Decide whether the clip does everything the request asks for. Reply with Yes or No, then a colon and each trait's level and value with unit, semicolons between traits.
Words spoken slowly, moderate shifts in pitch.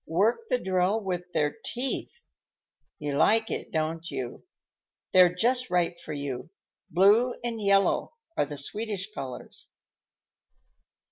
No: slow, 125 wpm; wide, 6.0 semitones